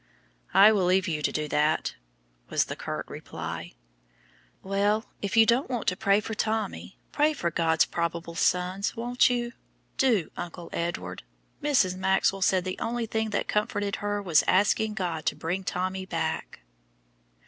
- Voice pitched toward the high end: Yes, high, 195 Hz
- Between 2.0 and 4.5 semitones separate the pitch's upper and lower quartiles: Yes, average, 3.8 semitones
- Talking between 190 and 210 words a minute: No, average, 160 wpm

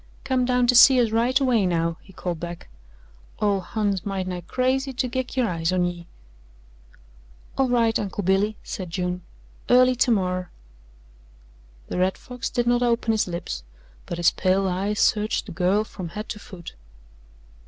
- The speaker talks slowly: No, average, 165 wpm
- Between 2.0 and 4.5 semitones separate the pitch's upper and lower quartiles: No, average, 5.1 semitones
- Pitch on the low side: No, high, 205 Hz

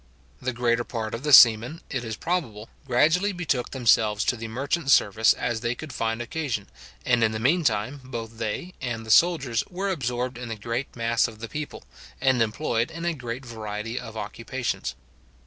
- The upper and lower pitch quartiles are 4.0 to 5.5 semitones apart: No, average, 3.6 semitones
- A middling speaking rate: Yes, average, 185 wpm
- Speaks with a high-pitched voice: No, low, 120 Hz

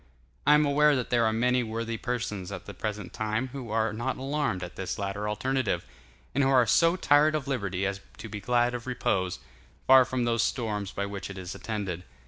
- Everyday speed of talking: No, fast, 210 wpm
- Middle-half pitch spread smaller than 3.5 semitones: No, average, 4.4 semitones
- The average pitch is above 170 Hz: No, low, 115 Hz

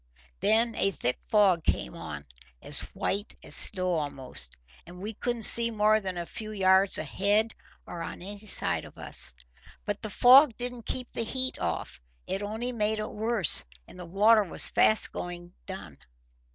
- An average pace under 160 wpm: No, average, 170 wpm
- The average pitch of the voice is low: No, high, 205 Hz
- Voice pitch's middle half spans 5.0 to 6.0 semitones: No, average, 3.7 semitones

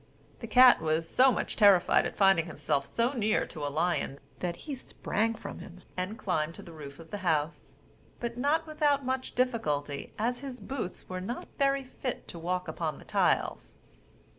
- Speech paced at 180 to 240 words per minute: Yes, average, 185 wpm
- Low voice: No, high, 195 Hz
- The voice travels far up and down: Yes, wide, 7.4 semitones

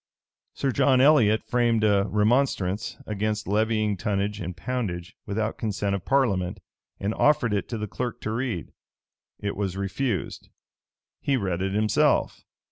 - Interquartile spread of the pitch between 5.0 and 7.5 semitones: No, average, 3.2 semitones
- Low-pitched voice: Yes, low, 105 Hz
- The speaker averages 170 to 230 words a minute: No, average, 140 wpm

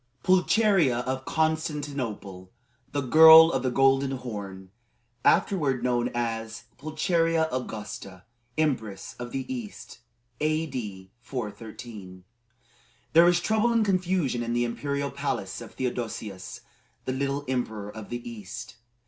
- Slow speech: Yes, slow, 115 wpm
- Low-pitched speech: Yes, low, 130 Hz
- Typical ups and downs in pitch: No, wide, 5.8 semitones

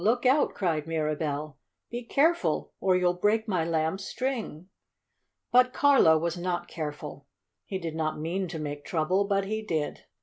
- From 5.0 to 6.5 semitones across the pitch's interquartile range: Yes, wide, 5.4 semitones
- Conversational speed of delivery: Yes, average, 160 wpm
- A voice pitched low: No, medium, 175 Hz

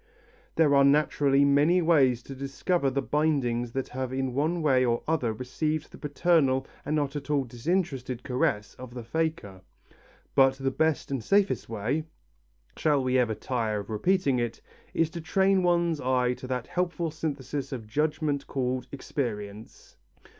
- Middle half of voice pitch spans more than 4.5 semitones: No, average, 3.9 semitones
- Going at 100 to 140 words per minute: No, average, 160 wpm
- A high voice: No, low, 135 Hz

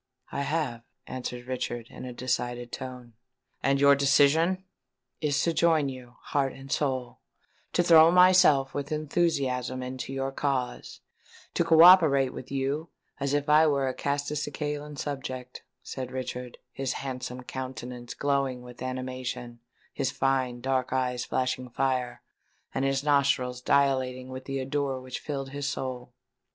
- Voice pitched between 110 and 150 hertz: Yes, low, 135 Hz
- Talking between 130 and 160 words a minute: Yes, average, 140 wpm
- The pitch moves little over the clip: Yes, narrow, 2.0 semitones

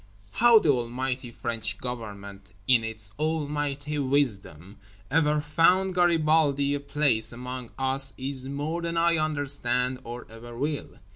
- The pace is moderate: No, slow, 130 wpm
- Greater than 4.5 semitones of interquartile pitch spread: No, average, 4.1 semitones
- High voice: No, low, 135 Hz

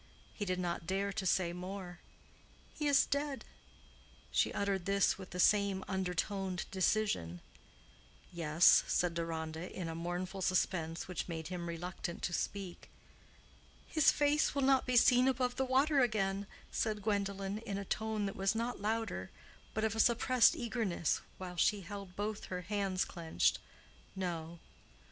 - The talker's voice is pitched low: No, high, 195 Hz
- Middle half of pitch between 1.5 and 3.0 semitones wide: No, average, 3.6 semitones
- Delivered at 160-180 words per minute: No, average, 150 wpm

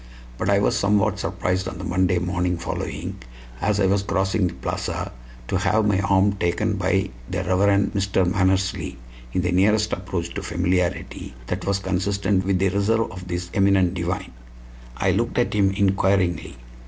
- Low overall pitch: Yes, very low, 95 Hz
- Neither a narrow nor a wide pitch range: No, narrow, 1.7 semitones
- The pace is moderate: Yes, average, 165 wpm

